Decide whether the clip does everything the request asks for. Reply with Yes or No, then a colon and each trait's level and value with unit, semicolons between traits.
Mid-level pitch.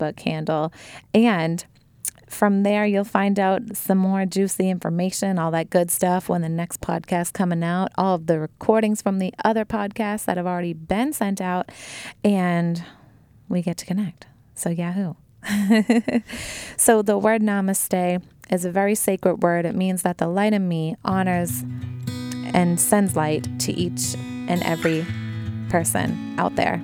Yes: medium, 180 Hz